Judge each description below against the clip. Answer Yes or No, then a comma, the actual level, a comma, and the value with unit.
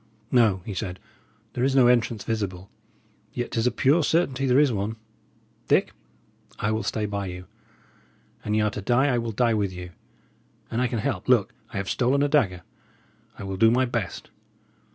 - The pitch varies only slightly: No, average, 4.0 semitones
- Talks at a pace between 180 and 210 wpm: Yes, average, 190 wpm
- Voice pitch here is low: Yes, low, 115 Hz